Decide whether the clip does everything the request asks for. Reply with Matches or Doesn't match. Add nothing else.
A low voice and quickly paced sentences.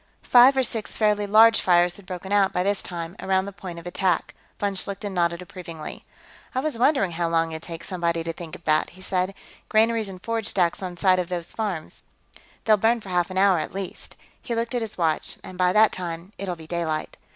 Doesn't match